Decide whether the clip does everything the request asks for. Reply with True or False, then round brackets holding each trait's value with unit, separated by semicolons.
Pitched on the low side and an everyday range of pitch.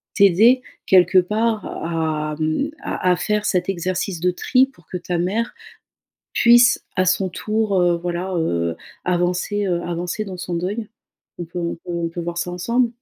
False (180 Hz; 3.3 semitones)